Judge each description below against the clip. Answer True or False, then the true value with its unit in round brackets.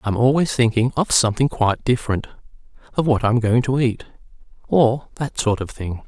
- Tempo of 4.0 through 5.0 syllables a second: False (5.5 syllables/s)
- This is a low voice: True (120 Hz)